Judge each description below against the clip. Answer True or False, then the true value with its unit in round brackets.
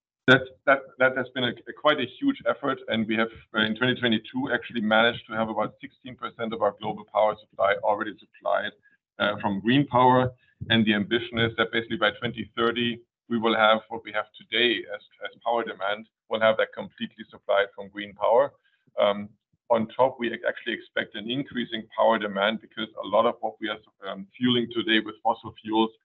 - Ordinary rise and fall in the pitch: False (2.0 semitones)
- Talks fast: False (190 wpm)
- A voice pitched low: True (115 Hz)